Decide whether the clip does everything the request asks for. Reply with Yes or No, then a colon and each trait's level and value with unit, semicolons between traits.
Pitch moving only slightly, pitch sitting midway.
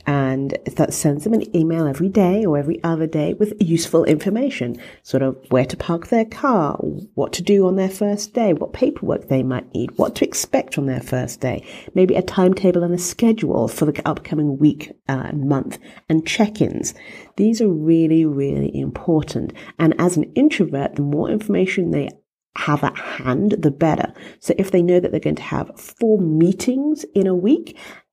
No: average, 5.2 semitones; medium, 170 Hz